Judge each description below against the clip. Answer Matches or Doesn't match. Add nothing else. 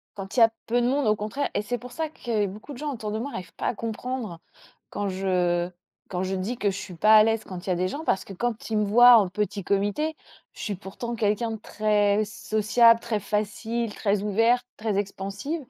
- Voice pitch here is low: Doesn't match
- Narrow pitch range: Doesn't match